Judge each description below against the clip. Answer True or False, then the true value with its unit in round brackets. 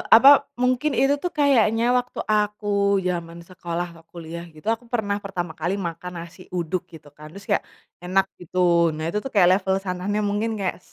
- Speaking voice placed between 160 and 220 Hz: True (190 Hz)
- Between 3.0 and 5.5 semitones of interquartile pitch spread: True (3.5 semitones)